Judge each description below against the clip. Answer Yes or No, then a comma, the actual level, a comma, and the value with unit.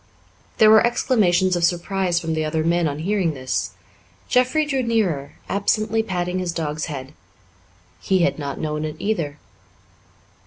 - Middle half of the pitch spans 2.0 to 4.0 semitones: No, average, 5.3 semitones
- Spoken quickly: No, average, 150 wpm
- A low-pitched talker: No, medium, 175 Hz